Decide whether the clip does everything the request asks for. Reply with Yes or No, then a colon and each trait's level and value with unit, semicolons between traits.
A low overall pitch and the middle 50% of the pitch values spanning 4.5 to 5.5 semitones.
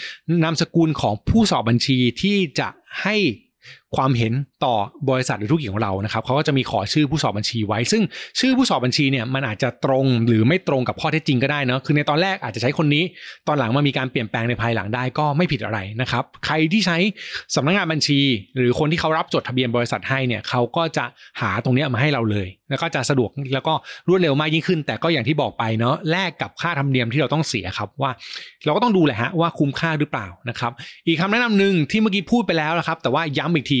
No: medium, 145 Hz; average, 4.8 semitones